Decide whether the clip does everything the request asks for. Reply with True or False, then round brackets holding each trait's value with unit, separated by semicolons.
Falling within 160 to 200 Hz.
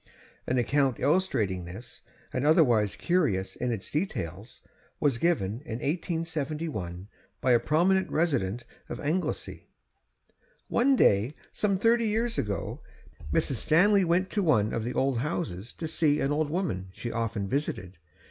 False (140 Hz)